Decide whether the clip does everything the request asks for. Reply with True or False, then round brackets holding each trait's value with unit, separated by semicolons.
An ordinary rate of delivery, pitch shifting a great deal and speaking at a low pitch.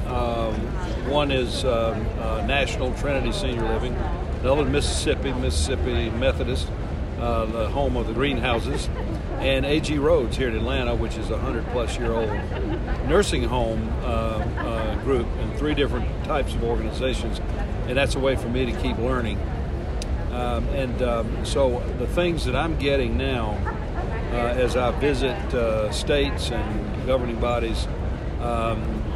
True (150 wpm; 6.6 semitones; 115 Hz)